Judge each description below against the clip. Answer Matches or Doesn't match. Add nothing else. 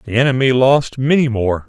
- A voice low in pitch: Matches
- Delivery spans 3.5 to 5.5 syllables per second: Matches